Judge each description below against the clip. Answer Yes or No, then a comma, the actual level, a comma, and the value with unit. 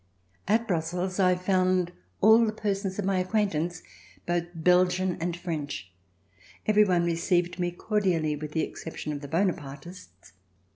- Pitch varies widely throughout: No, narrow, 2.5 semitones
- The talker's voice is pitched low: No, medium, 180 Hz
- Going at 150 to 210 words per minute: No, average, 140 wpm